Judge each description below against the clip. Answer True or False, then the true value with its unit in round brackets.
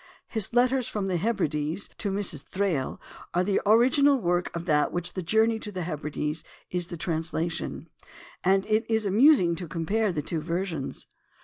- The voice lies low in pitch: False (185 Hz)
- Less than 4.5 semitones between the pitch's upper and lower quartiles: False (4.8 semitones)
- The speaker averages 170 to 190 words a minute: True (175 wpm)